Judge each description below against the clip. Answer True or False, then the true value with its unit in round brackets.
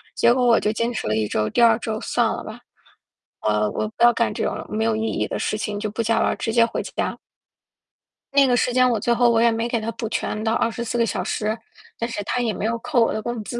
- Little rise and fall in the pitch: True (1.7 semitones)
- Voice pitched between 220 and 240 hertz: True (230 Hz)